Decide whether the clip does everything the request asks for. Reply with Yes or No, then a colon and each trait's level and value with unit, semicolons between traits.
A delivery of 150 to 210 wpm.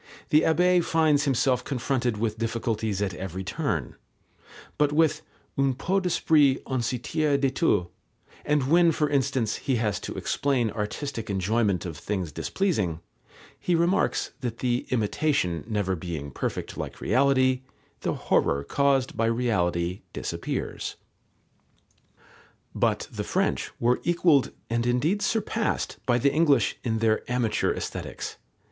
No: slow, 135 wpm